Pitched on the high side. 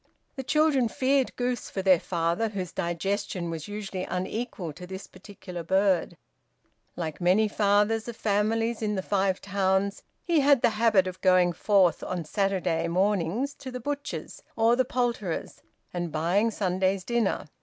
Yes: high, 200 Hz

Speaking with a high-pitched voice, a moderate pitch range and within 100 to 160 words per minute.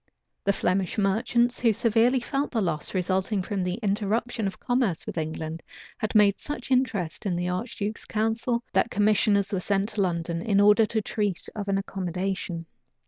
No: high, 200 Hz; average, 3.3 semitones; average, 170 wpm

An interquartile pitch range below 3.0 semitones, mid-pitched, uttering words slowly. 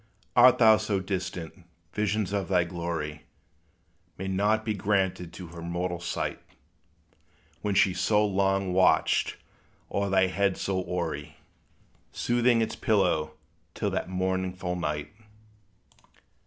No: narrow, 2.6 semitones; very low, 95 Hz; slow, 120 wpm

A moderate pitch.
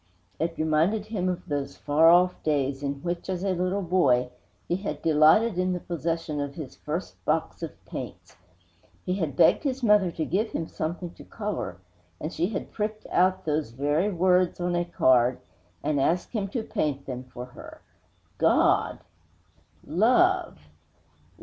Yes: medium, 170 Hz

